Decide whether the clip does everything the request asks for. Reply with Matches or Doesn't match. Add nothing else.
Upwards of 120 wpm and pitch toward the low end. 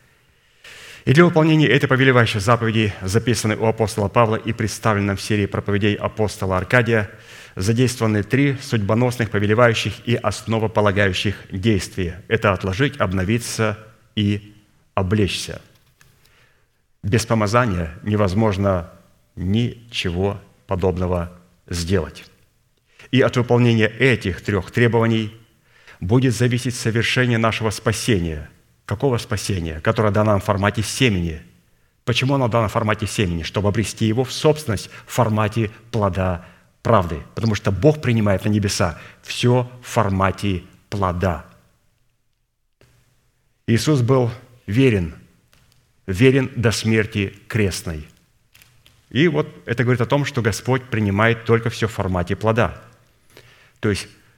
Doesn't match